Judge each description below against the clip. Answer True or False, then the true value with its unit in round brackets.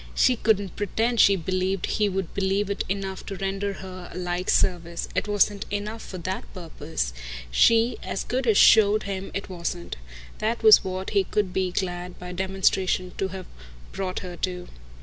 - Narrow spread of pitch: True (2.0 semitones)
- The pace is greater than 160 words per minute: True (175 wpm)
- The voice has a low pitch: False (190 Hz)